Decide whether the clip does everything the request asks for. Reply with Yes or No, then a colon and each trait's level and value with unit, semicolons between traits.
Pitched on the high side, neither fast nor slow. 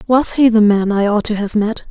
No: high, 215 Hz; fast, 285 wpm